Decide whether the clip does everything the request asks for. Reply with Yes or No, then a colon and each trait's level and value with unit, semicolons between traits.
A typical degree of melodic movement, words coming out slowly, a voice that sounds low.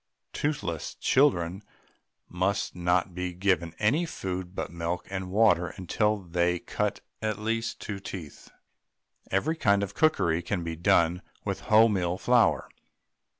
Yes: average, 3.5 semitones; slow, 130 wpm; very low, 95 Hz